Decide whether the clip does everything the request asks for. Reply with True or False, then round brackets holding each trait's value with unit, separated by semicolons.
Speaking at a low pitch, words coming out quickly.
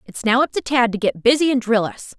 False (240 Hz; 305 wpm)